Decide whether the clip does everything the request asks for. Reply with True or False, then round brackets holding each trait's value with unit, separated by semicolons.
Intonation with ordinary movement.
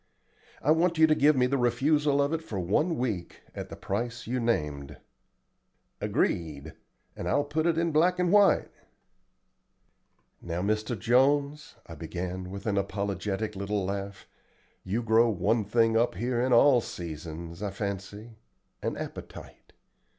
False (6.6 semitones)